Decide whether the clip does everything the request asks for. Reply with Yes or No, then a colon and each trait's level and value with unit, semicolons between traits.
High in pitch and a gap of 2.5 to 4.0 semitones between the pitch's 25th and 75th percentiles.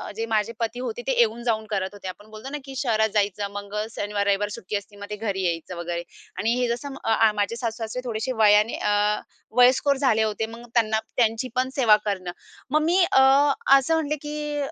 Yes: high, 220 Hz; average, 3.5 semitones